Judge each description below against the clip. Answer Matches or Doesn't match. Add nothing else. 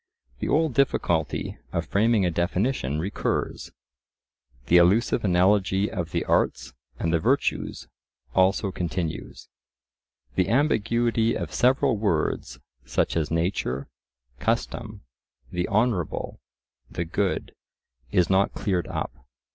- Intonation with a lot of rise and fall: Doesn't match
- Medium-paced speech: Doesn't match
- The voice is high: Doesn't match